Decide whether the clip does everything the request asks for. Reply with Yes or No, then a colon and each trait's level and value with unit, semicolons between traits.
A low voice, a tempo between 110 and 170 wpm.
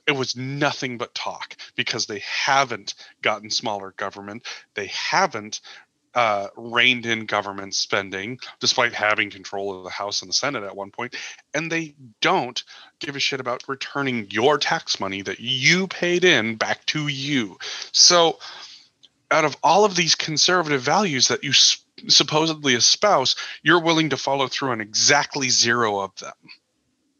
Yes: low, 130 Hz; average, 155 wpm